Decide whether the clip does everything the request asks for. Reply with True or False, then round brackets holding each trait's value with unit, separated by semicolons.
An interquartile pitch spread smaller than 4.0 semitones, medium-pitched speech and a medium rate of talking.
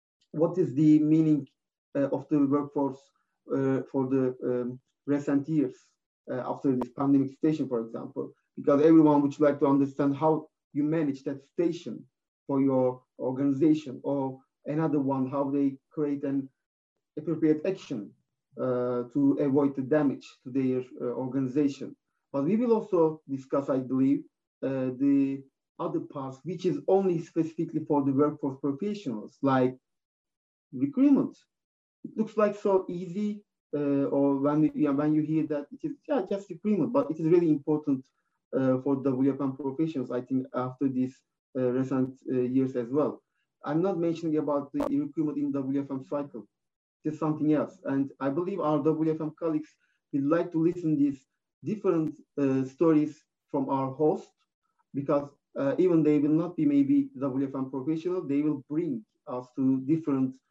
True (3.2 semitones; 145 Hz; 160 wpm)